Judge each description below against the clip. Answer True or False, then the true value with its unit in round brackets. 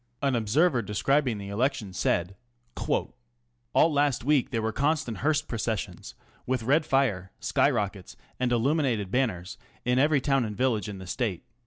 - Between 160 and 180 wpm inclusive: True (165 wpm)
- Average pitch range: True (5.0 semitones)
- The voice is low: True (125 Hz)